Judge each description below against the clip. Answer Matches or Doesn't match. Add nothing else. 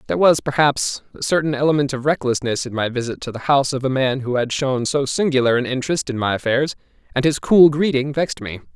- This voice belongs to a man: Matches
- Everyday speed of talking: Doesn't match